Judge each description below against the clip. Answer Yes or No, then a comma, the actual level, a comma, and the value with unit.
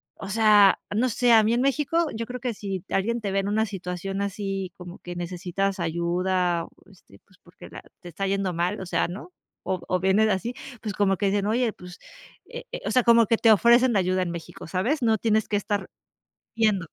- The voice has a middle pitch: No, high, 200 Hz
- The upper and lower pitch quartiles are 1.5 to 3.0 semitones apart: No, average, 3.6 semitones